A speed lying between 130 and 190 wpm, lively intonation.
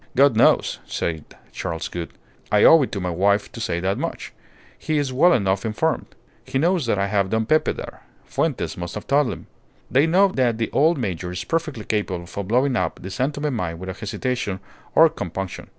No: average, 200 wpm; wide, 7.0 semitones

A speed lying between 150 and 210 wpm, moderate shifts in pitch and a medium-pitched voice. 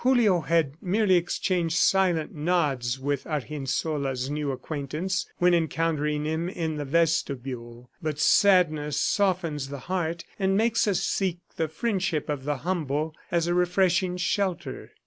No: slow, 135 wpm; average, 3.6 semitones; medium, 165 Hz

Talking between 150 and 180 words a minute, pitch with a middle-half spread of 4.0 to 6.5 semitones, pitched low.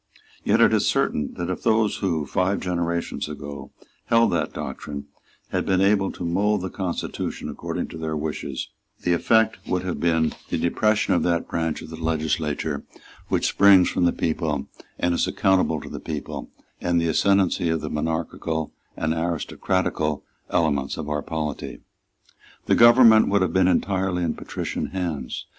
No: average, 165 wpm; average, 3.2 semitones; very low, 85 Hz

